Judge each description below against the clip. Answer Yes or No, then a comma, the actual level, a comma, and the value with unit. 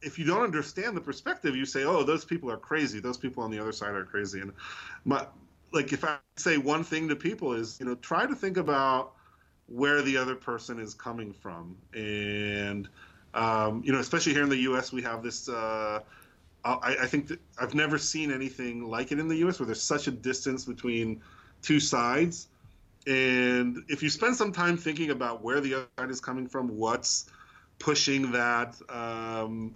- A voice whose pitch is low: Yes, low, 130 Hz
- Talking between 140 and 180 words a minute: No, average, 200 wpm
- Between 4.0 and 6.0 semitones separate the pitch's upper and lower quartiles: Yes, average, 4.6 semitones